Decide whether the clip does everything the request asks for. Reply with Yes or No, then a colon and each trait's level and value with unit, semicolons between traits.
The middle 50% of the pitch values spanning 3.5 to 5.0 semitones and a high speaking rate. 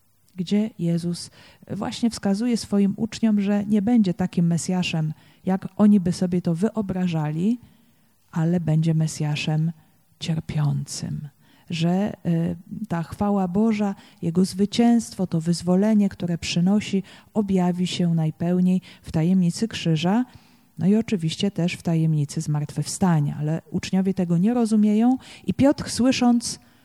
No: average, 4.0 semitones; average, 120 wpm